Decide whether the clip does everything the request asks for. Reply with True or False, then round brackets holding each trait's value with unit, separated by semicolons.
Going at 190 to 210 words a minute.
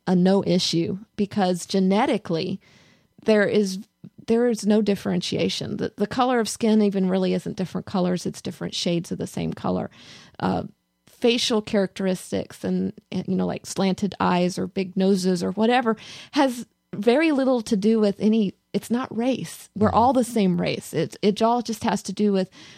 False (170 wpm)